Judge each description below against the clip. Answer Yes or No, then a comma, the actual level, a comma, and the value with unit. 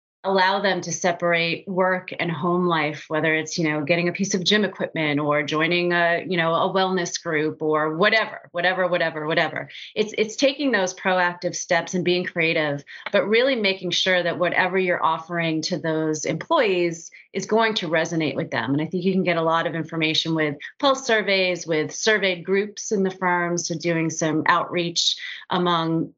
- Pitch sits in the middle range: Yes, medium, 175 Hz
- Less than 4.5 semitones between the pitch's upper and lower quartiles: Yes, narrow, 2.5 semitones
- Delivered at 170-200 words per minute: Yes, average, 185 wpm